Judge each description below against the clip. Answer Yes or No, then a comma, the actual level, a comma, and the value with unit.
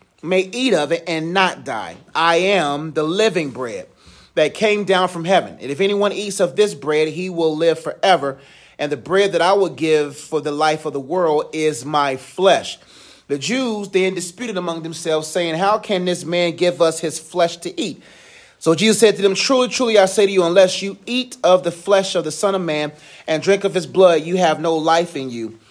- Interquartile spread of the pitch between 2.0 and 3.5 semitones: No, average, 3.9 semitones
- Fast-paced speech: Yes, fast, 220 wpm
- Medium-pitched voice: Yes, medium, 175 Hz